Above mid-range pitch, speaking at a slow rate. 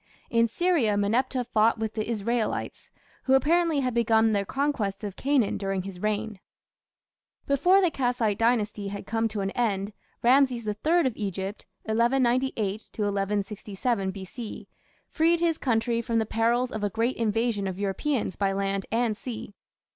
No: high, 225 Hz; average, 150 wpm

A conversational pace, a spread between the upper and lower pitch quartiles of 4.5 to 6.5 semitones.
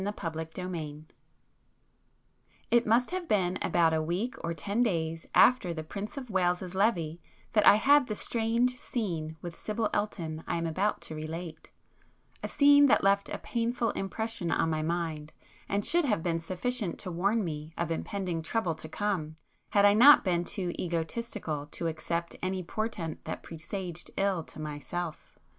Yes: average, 165 wpm; average, 4.8 semitones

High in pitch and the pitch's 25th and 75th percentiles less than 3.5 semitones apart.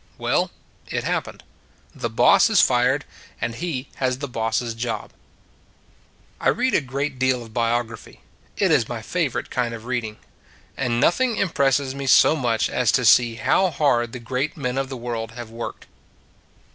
No: low, 125 Hz; average, 2.8 semitones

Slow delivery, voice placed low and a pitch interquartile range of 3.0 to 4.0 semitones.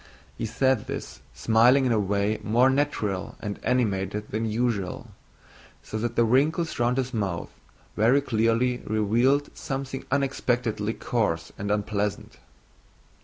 Yes: slow, 125 wpm; low, 115 Hz; average, 3.6 semitones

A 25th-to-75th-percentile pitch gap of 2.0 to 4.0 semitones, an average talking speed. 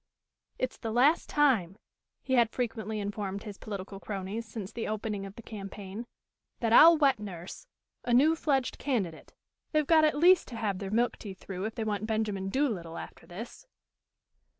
No: average, 4.5 semitones; average, 175 wpm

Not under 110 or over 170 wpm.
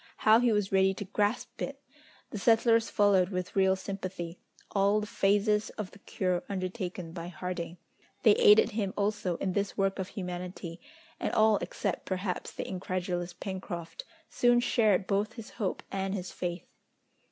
Yes: average, 160 wpm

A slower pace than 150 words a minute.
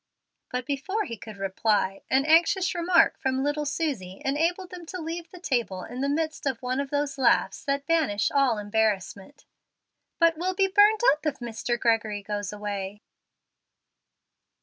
No: average, 155 wpm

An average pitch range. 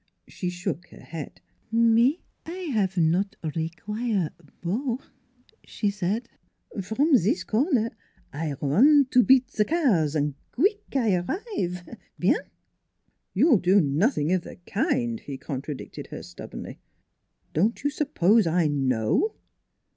No: wide, 7.5 semitones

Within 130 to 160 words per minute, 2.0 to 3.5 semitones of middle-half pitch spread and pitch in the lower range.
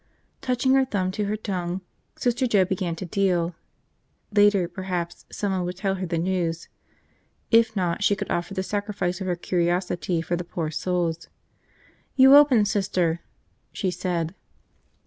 No: average, 150 wpm; average, 2.9 semitones; medium, 185 Hz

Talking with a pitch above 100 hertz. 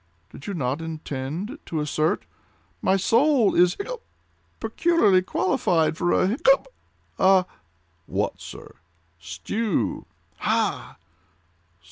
Yes: medium, 185 Hz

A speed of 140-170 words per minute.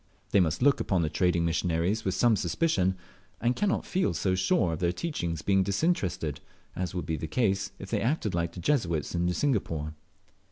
No: average, 190 wpm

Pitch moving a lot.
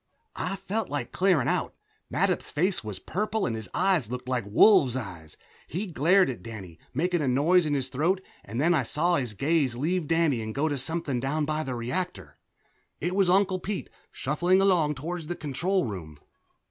Yes: wide, 6.3 semitones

